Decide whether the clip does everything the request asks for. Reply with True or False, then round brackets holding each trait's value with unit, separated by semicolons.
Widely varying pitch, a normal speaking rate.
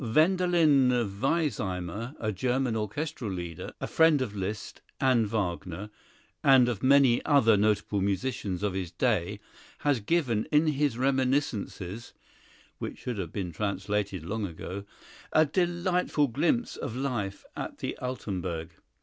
False (5.8 semitones; 130 wpm)